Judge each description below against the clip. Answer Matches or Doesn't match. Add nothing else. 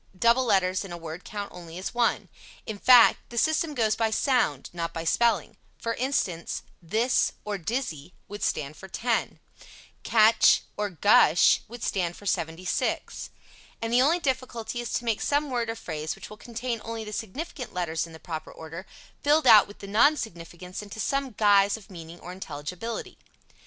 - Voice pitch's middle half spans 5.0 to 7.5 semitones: Matches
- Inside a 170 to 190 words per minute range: Matches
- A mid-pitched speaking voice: Doesn't match